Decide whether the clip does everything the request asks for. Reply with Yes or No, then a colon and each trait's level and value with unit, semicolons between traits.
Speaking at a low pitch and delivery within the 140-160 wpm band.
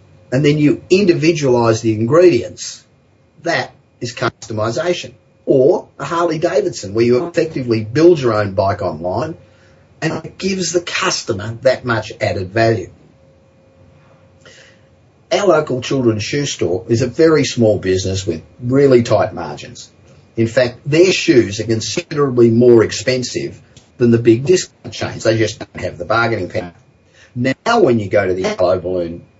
Yes: low, 120 Hz; average, 145 wpm